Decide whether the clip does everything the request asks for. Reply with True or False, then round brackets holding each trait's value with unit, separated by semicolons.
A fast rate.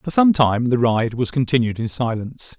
True (210 wpm)